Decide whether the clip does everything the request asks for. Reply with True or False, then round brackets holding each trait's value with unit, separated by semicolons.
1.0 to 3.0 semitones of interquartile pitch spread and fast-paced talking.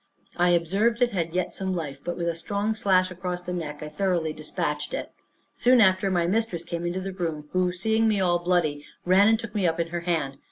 True (2.6 semitones; 230 wpm)